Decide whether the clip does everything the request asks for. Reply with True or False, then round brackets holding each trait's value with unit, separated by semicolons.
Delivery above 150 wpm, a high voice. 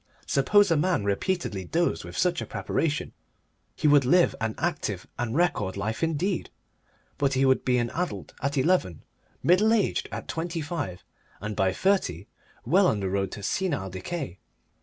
False (165 wpm; 140 Hz)